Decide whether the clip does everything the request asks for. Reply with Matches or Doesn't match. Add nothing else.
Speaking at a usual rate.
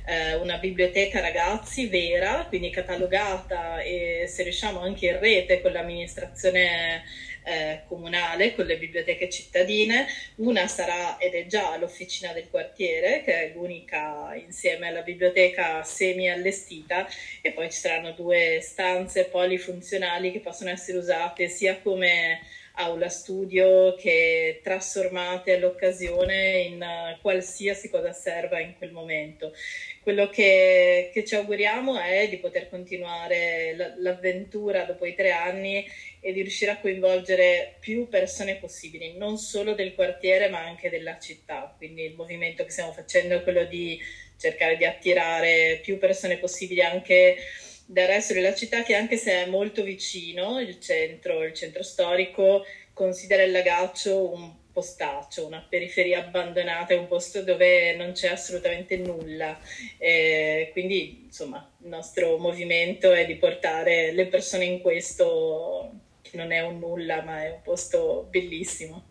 Matches